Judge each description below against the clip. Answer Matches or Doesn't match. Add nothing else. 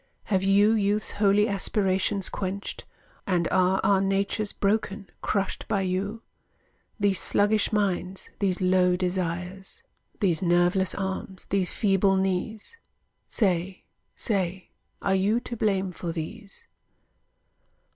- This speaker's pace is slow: Matches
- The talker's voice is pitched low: Doesn't match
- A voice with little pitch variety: Matches